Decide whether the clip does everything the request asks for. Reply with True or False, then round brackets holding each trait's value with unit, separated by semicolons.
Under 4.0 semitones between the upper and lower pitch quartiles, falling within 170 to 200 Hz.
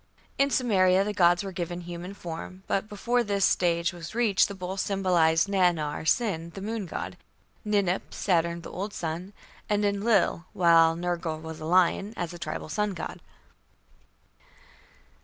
True (2.9 semitones; 185 Hz)